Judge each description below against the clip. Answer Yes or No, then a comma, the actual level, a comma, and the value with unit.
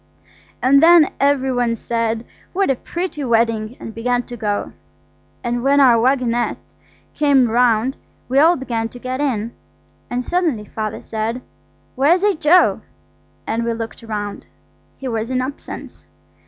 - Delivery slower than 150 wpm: Yes, average, 140 wpm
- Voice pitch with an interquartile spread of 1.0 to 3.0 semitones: No, average, 3.4 semitones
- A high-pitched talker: Yes, high, 245 Hz